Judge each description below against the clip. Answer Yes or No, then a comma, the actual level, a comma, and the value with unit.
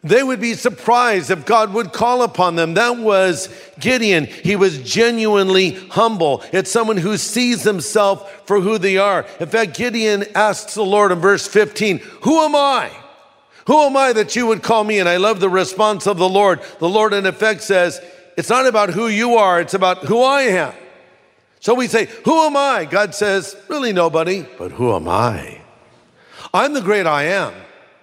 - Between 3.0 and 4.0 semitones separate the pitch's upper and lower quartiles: Yes, average, 3.3 semitones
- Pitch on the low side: No, high, 205 Hz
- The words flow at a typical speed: Yes, average, 190 wpm